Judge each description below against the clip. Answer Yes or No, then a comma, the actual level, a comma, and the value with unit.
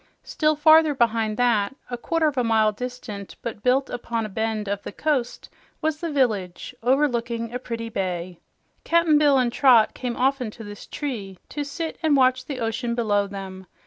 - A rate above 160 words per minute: Yes, average, 180 wpm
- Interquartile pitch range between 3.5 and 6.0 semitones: Yes, average, 4.5 semitones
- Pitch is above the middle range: Yes, high, 240 Hz